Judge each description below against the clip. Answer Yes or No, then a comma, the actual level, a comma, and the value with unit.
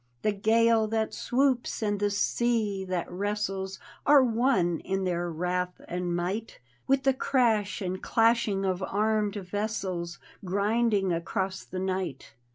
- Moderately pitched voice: No, high, 200 Hz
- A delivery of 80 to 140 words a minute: Yes, slow, 135 wpm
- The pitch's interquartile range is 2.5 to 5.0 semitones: Yes, average, 3.5 semitones